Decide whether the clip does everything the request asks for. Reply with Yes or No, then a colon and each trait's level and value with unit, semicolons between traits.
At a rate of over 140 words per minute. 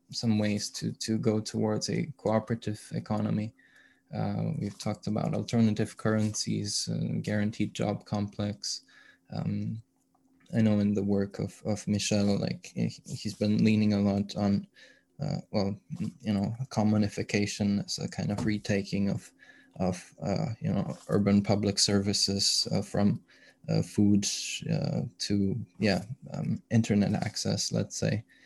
No: slow, 135 wpm